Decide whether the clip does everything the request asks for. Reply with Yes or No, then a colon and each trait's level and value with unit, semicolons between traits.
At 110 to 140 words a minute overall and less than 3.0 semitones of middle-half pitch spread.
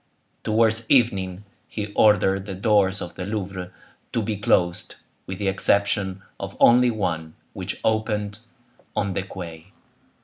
Yes: slow, 135 wpm; narrow, 2.5 semitones